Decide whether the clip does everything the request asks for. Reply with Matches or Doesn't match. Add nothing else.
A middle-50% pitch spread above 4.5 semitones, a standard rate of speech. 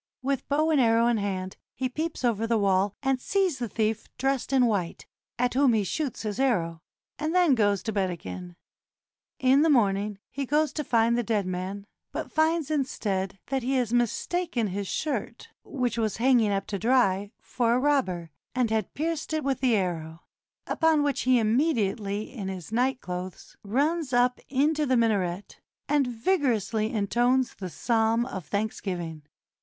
Matches